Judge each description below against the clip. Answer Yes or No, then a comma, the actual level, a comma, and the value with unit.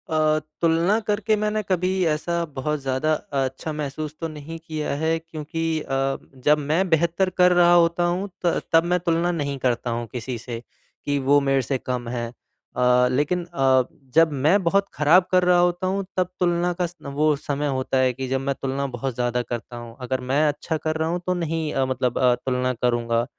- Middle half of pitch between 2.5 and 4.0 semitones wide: No, average, 4.7 semitones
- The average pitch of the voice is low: No, medium, 155 Hz